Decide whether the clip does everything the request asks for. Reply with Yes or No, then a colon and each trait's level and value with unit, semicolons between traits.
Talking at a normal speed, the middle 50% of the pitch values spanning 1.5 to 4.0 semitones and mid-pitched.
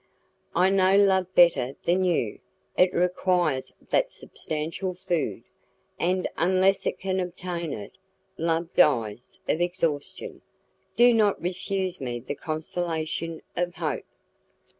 No: slow, 120 wpm; average, 2.9 semitones; medium, 175 Hz